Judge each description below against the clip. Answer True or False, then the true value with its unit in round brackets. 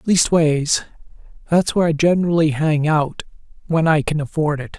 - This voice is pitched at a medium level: True (155 Hz)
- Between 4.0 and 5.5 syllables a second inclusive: True (5.1 syllables/s)